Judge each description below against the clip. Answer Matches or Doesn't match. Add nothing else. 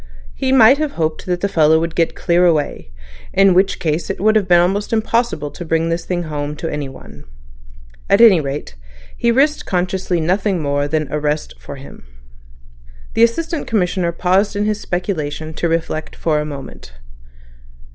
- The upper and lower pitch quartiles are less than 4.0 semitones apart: Doesn't match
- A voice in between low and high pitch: Matches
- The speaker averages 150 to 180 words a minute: Matches